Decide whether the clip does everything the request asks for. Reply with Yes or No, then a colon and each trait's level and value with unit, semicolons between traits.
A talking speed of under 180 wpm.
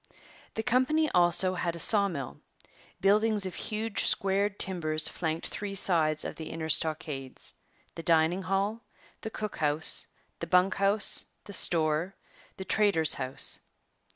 Yes: average, 140 wpm